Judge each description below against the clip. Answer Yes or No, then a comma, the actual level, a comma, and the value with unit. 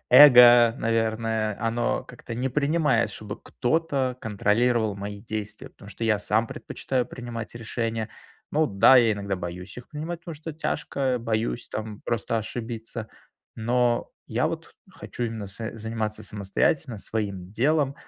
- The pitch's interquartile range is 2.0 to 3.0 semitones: Yes, narrow, 2.6 semitones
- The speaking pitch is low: Yes, low, 115 Hz